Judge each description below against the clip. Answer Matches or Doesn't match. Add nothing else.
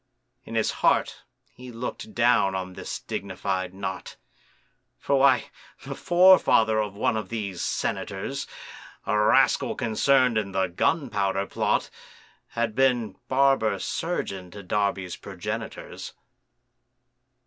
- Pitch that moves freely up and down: Doesn't match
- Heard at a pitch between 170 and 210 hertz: Doesn't match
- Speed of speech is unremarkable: Doesn't match